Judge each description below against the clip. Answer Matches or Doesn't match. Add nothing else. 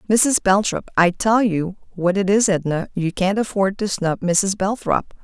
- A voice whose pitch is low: Doesn't match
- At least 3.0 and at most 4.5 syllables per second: Matches